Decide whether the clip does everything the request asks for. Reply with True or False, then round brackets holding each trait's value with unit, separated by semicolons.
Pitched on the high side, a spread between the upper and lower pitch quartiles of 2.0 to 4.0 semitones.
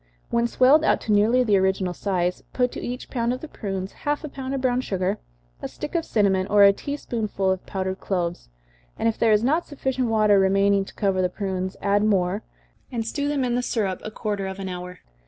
False (205 Hz; 4.6 semitones)